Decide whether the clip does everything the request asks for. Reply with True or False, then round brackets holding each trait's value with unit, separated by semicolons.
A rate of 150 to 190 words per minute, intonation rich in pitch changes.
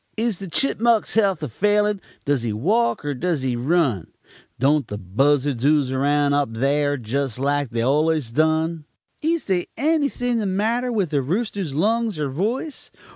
True (165 wpm; 7.2 semitones)